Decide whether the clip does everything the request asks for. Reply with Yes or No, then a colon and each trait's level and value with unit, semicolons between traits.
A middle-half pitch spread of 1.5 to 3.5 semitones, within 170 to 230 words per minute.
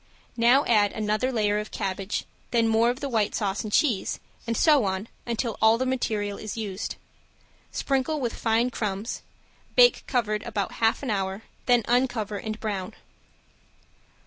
No: average, 2.9 semitones; average, 155 wpm